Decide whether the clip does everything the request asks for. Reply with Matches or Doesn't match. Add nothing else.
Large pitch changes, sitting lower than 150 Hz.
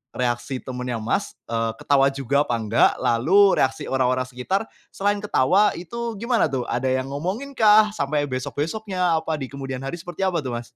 Matches